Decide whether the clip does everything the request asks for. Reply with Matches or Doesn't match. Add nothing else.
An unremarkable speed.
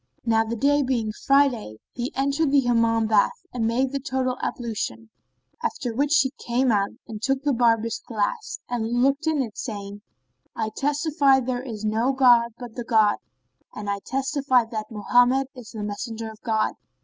Matches